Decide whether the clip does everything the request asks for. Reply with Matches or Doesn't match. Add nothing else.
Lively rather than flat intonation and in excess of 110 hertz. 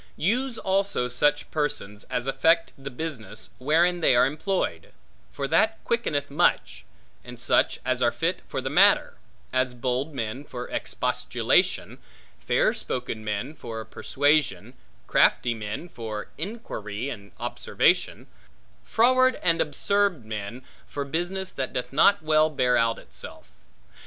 Matches